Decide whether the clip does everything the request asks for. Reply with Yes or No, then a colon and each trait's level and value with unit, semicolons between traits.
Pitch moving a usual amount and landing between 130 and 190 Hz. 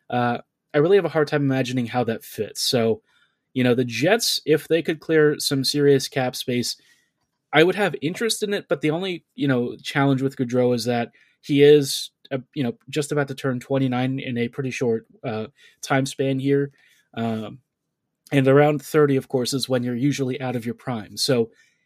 Yes: average, 3.1 semitones; low, 135 Hz